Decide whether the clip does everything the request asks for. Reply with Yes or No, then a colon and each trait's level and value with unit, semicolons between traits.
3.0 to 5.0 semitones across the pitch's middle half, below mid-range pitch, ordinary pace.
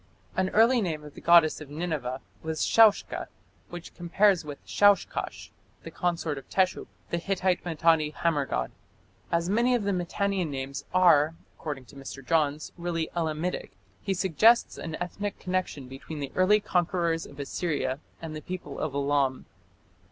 No: average, 4.0 semitones; medium, 165 Hz; average, 155 wpm